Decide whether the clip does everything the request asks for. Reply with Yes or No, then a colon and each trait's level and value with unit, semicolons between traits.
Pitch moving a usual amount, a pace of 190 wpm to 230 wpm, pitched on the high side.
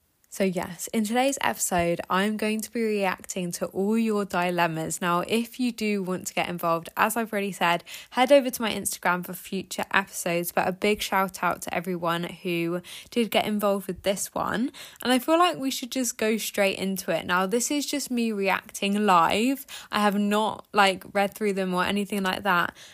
Yes: average, 3.5 semitones; average, 200 wpm; high, 200 Hz